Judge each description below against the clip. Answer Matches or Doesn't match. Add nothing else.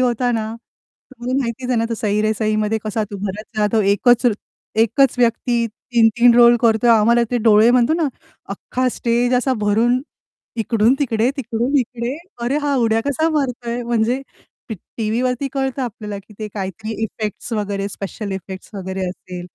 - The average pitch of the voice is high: Matches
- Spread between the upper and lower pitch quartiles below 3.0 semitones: Matches